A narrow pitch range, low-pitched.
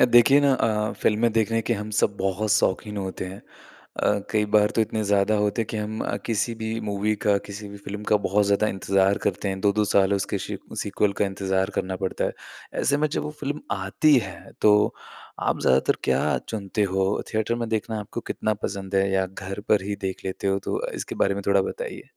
Yes: narrow, 1.9 semitones; low, 105 Hz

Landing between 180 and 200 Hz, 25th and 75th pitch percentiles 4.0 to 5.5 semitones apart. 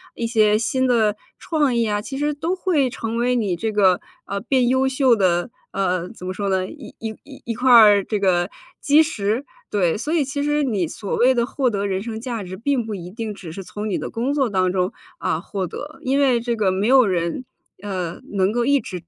No: high, 225 Hz; average, 5.0 semitones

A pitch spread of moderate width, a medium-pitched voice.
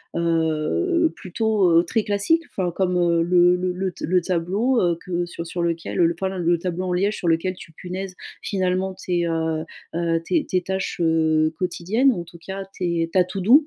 No: narrow, 2.3 semitones; medium, 180 Hz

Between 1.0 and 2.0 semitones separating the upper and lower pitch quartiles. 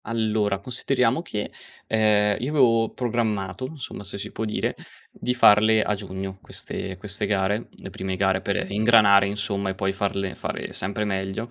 No: narrow, 2.6 semitones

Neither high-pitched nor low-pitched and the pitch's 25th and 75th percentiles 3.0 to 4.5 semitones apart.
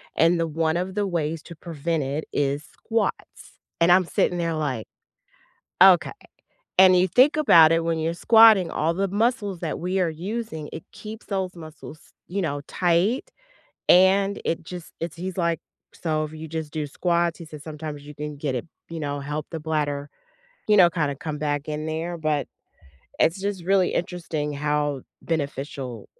Yes: medium, 165 Hz; average, 3.3 semitones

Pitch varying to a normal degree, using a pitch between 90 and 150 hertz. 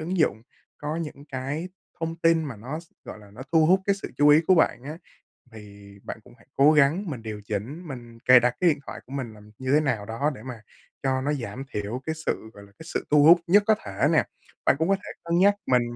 No: wide, 5.9 semitones; medium, 140 Hz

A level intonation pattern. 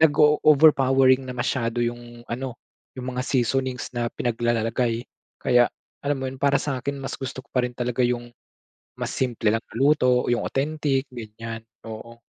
Yes: narrow, 2.2 semitones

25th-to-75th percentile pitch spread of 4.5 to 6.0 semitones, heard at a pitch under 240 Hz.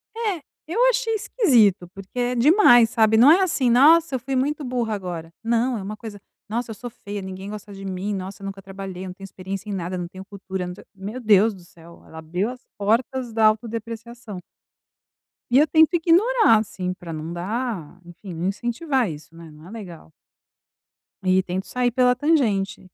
Yes: average, 4.9 semitones; high, 215 Hz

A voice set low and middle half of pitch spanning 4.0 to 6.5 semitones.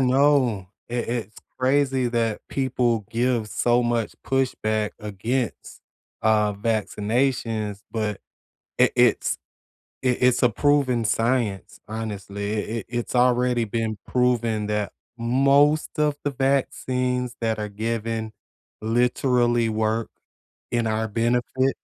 No: low, 120 Hz; narrow, 2.6 semitones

